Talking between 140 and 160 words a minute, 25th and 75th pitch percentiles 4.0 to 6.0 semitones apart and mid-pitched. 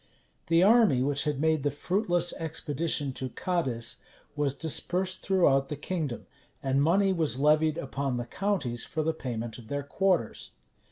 Yes: average, 155 wpm; average, 4.4 semitones; medium, 150 Hz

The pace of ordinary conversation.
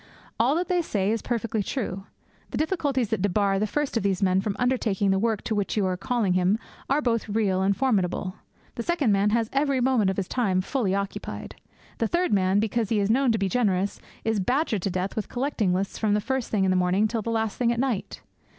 No: fast, 230 wpm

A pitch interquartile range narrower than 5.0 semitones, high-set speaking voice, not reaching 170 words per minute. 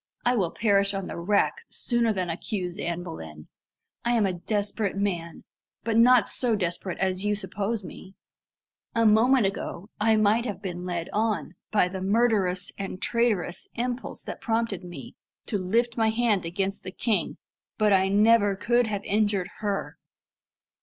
Yes: average, 3.4 semitones; high, 205 Hz; average, 160 wpm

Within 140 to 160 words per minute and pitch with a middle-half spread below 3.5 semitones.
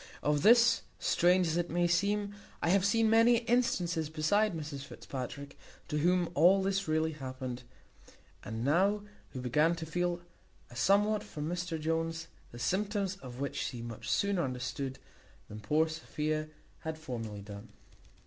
No: average, 150 wpm; wide, 5.5 semitones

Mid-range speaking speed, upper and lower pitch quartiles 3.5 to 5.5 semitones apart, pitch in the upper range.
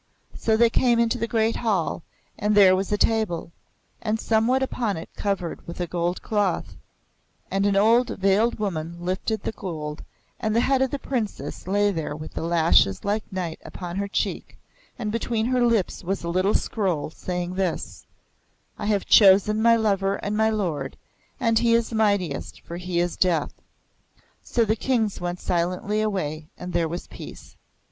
Yes: average, 175 wpm; average, 4.0 semitones; high, 200 Hz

